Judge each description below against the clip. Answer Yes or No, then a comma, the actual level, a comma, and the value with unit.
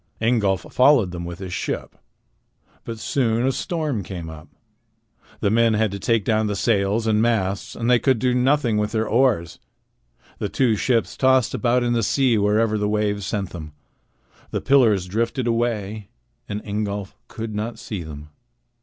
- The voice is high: No, low, 110 Hz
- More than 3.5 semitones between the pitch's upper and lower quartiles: No, average, 3.0 semitones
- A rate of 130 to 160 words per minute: No, average, 170 wpm